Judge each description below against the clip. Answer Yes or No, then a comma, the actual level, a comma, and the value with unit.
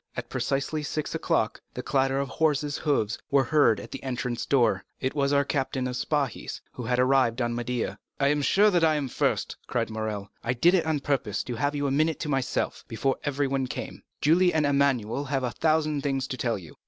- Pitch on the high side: No, low, 135 Hz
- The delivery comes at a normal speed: No, fast, 215 wpm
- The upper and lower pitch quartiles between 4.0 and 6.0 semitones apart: No, average, 2.8 semitones